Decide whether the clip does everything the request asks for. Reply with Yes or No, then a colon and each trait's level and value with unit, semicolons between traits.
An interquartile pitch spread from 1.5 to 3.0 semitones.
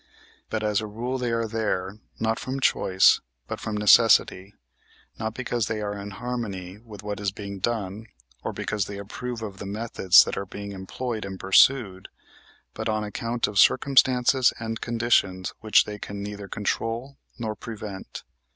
Yes: narrow, 2.5 semitones